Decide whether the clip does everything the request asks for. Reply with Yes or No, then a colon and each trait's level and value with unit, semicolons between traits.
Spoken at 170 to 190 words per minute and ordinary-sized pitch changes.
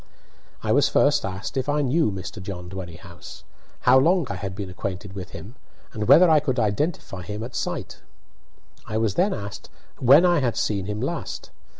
No: average, 185 wpm; wide, 6.2 semitones